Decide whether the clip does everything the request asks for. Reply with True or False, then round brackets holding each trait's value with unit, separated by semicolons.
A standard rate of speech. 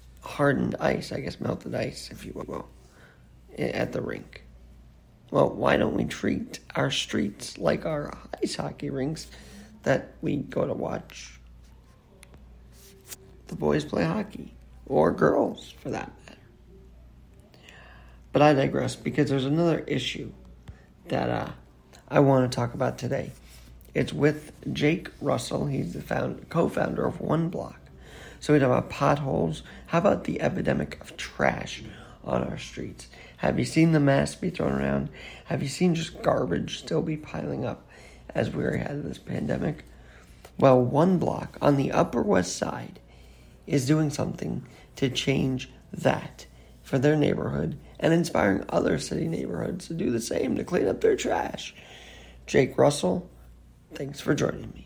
True (150 wpm)